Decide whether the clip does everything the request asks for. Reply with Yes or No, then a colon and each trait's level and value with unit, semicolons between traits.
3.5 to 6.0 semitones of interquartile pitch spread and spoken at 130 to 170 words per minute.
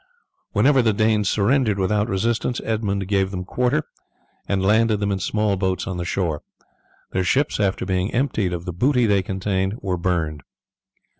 No: average, 3.0 semitones; average, 165 wpm